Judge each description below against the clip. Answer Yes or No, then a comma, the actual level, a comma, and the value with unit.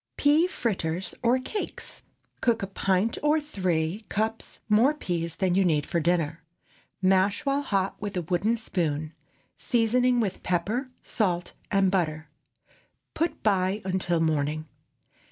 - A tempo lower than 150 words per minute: Yes, slow, 135 wpm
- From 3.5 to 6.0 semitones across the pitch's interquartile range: Yes, average, 5.2 semitones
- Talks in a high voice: Yes, high, 195 Hz